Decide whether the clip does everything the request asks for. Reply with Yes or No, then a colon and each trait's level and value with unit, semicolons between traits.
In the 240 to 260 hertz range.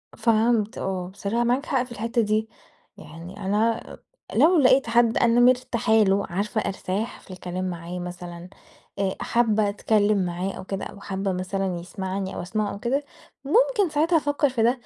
No: high, 210 Hz